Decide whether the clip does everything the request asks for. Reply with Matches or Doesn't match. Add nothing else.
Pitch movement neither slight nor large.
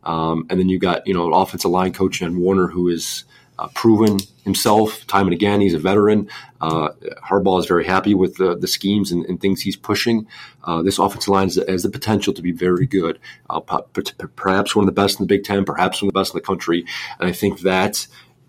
Doesn't match